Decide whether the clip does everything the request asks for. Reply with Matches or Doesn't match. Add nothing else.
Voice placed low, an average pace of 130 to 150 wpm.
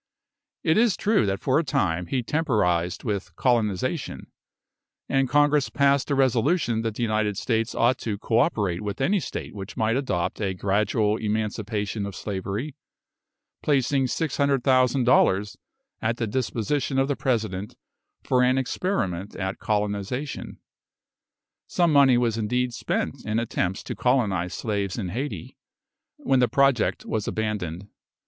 Matches